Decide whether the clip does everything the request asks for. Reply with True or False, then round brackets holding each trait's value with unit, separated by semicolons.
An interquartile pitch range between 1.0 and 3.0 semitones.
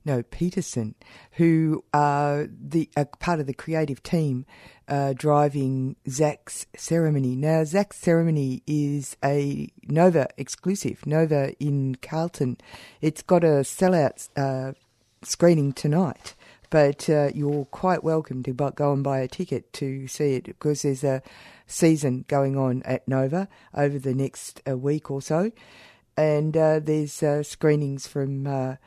True (2.7 semitones)